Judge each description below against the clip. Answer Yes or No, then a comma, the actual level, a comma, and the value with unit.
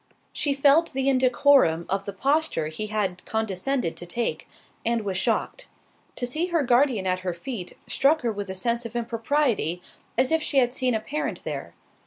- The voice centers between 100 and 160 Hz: No, high, 235 Hz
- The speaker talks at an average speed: Yes, average, 185 wpm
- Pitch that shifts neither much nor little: No, wide, 6.0 semitones